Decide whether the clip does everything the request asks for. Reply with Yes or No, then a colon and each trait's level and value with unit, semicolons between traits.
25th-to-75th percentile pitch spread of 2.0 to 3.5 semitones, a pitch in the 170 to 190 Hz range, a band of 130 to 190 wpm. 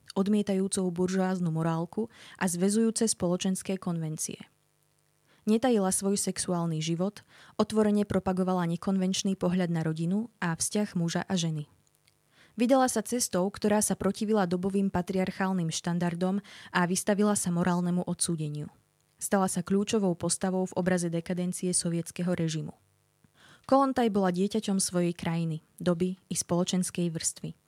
No: narrow, 2.4 semitones; medium, 185 Hz; average, 115 wpm